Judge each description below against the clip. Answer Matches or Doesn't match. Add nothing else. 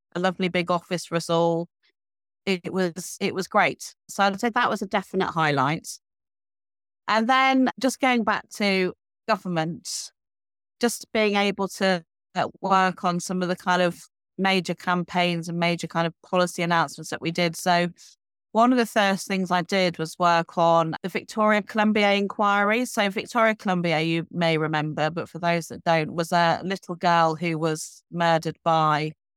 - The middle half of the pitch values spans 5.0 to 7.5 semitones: Doesn't match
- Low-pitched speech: Doesn't match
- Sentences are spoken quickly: Doesn't match